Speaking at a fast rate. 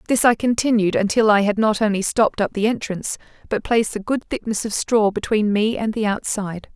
Yes: fast, 215 wpm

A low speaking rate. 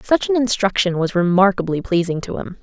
No: average, 185 wpm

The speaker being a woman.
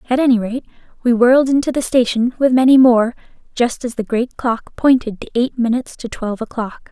Yes: female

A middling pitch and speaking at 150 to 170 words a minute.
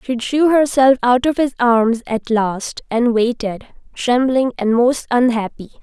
No: high, 245 Hz; average, 155 wpm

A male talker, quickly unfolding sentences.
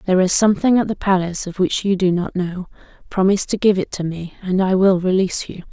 No: female; fast, 240 wpm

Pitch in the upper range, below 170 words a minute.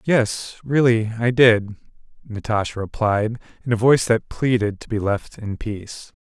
No: low, 110 Hz; average, 155 wpm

